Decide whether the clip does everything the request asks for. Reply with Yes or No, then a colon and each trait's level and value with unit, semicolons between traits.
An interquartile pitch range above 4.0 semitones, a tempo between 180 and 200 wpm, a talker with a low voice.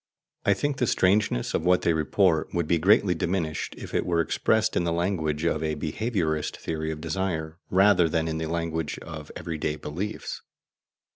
No: average, 3.2 semitones; average, 185 wpm; very low, 85 Hz